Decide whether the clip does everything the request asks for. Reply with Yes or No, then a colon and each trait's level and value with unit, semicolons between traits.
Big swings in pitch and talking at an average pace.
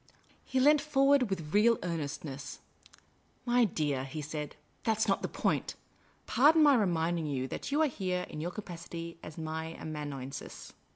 Yes: wide, 7.5 semitones; average, 170 wpm